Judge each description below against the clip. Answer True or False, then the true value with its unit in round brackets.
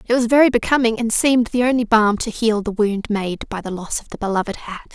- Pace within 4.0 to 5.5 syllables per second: False (5.9 syllables/s)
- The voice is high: True (220 Hz)